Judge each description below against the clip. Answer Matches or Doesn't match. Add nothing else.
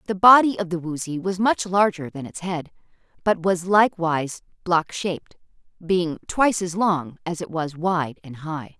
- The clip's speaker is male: Doesn't match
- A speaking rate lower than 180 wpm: Matches